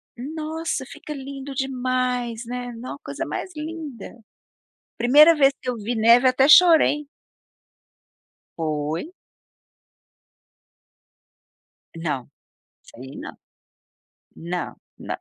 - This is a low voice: No, very high, 255 Hz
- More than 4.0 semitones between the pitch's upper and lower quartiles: Yes, average, 4.5 semitones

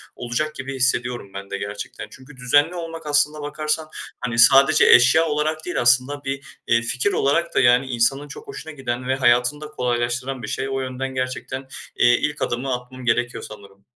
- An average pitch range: Yes, average, 3.3 semitones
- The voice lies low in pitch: Yes, low, 130 Hz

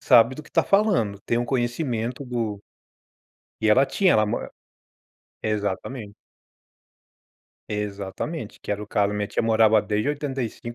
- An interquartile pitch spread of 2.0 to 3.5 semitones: No, average, 4.0 semitones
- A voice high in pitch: No, low, 115 Hz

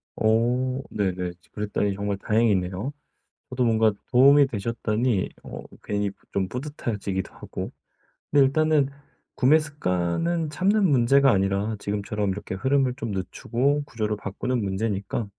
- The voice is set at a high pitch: No, low, 115 Hz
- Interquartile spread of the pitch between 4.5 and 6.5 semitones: Yes, average, 5.2 semitones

